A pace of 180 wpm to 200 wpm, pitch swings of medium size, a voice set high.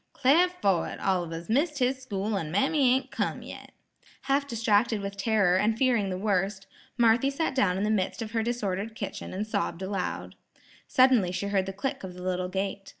Yes: average, 195 wpm; average, 4.4 semitones; high, 205 Hz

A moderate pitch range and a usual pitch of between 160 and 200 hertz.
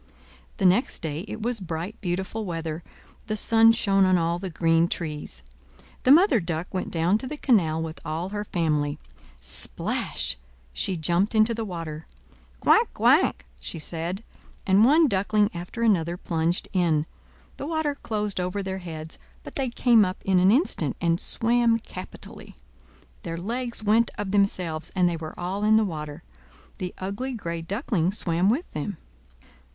Yes: average, 4.7 semitones; medium, 185 Hz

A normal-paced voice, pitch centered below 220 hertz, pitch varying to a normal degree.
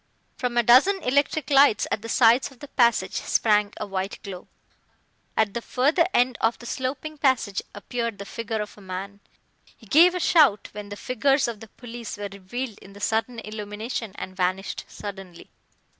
No: average, 180 wpm; high, 225 Hz; average, 4.0 semitones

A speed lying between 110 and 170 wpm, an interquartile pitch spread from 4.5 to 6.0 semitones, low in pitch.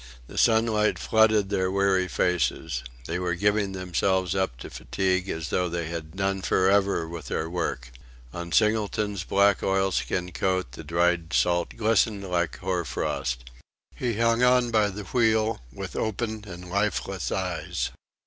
No: average, 150 wpm; average, 3.4 semitones; very low, 95 Hz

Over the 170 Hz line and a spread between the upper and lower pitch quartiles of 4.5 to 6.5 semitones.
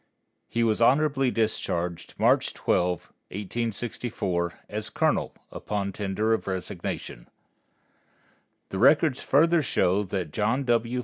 No: low, 110 Hz; average, 4.8 semitones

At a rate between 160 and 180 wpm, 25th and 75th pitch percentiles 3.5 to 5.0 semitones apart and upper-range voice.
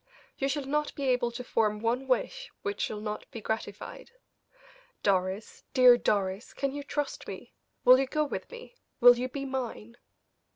Yes: average, 170 wpm; average, 3.8 semitones; very high, 250 Hz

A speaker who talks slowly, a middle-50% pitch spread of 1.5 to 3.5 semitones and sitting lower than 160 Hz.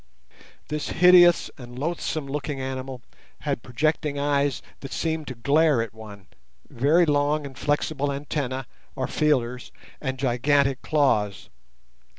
Yes: slow, 125 wpm; average, 2.8 semitones; medium, 140 Hz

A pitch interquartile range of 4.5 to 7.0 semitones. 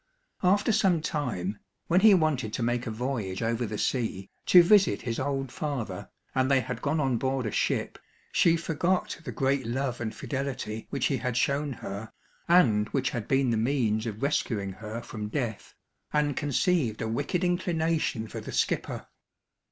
Yes: average, 5.1 semitones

